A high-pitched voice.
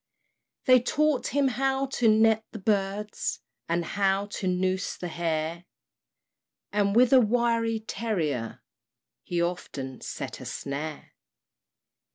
Yes: high, 205 Hz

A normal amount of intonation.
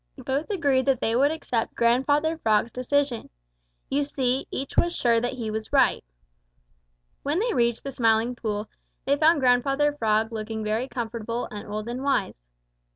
Yes: average, 3.9 semitones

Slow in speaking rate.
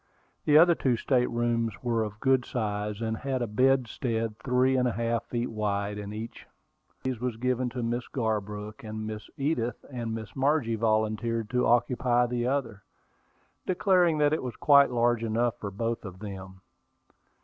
No: average, 175 wpm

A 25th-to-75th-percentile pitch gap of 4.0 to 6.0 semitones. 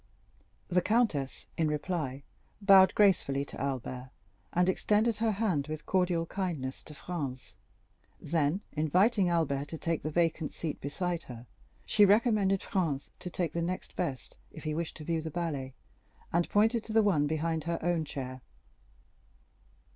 Yes: average, 4.4 semitones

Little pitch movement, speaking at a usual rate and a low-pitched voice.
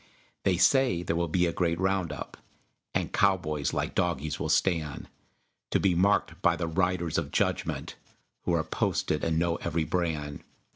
Yes: narrow, 2.1 semitones; average, 165 wpm; very low, 85 Hz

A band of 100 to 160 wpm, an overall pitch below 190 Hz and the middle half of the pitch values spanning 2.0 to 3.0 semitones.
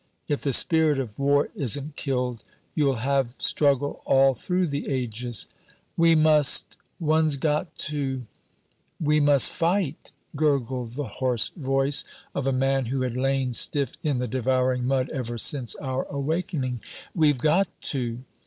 Yes: average, 145 wpm; low, 135 Hz; average, 2.7 semitones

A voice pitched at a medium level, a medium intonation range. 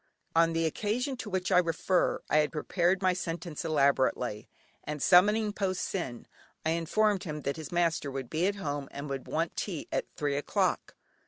Yes: medium, 165 Hz; average, 4.0 semitones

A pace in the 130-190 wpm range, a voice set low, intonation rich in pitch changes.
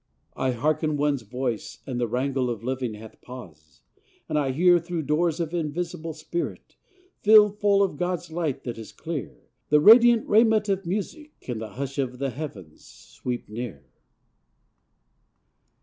No: average, 150 wpm; medium, 150 Hz; wide, 6.0 semitones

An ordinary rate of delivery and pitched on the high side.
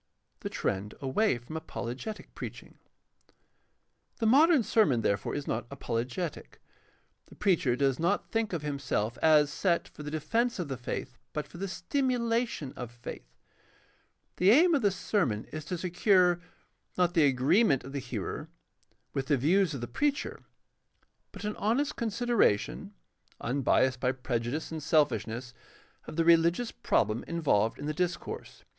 No: average, 150 wpm; medium, 155 Hz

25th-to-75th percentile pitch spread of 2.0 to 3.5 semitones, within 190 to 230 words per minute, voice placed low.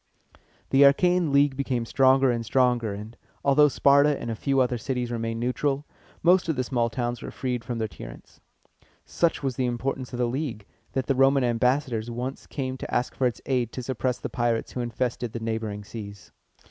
Yes: narrow, 2.5 semitones; average, 195 wpm; low, 125 Hz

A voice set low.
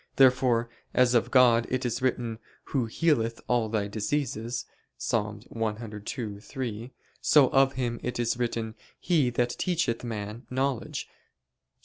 Yes: low, 120 Hz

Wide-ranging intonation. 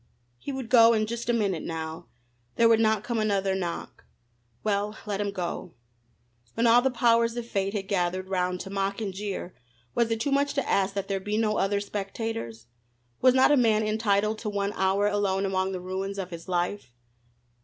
No: average, 3.0 semitones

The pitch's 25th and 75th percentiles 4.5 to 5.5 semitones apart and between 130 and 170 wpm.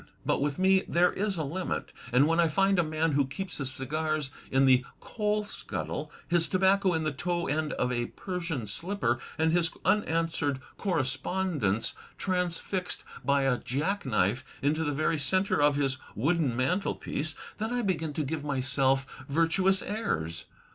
Yes: average, 5.1 semitones; average, 160 wpm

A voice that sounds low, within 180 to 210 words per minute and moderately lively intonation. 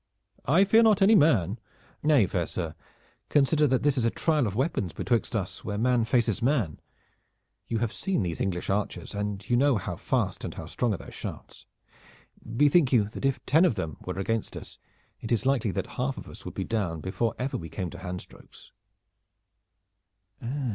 No: low, 115 Hz; average, 190 wpm; wide, 6.1 semitones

